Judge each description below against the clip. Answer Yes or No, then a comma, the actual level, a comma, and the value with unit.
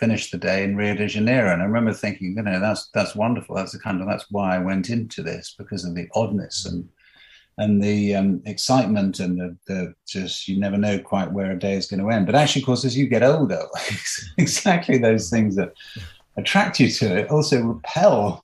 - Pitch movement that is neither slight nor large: Yes, average, 3.0 semitones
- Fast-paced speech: Yes, fast, 220 wpm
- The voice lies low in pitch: Yes, low, 100 Hz